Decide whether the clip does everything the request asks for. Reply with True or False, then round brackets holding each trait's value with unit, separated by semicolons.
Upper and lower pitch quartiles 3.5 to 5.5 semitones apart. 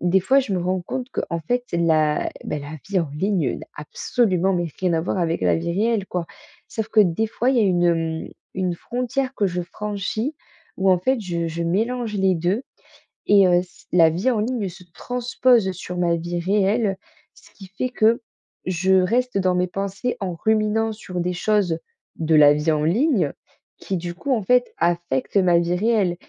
True (4.3 semitones)